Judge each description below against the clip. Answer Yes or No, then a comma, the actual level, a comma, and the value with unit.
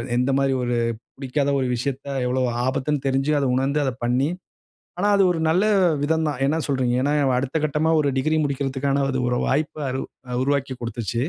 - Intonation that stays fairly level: Yes, narrow, 2.1 semitones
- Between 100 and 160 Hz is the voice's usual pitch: Yes, low, 135 Hz